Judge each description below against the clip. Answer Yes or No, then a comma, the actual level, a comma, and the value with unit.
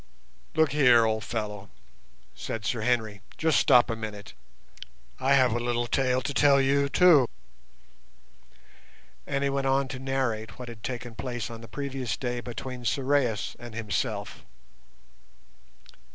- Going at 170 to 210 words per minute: No, average, 140 wpm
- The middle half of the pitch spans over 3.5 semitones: No, average, 3.2 semitones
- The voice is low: Yes, low, 125 Hz